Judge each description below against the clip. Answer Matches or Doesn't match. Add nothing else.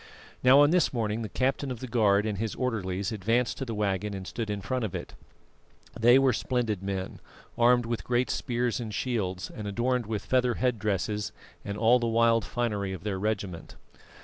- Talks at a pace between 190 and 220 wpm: Matches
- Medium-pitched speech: Doesn't match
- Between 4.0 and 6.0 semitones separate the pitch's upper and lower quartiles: Doesn't match